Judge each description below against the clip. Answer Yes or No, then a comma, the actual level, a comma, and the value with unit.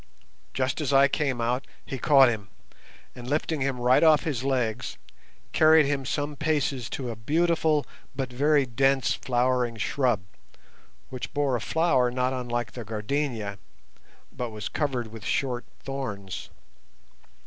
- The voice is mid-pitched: No, low, 130 Hz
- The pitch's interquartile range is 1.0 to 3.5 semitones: Yes, average, 3.0 semitones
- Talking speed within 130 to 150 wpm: Yes, average, 140 wpm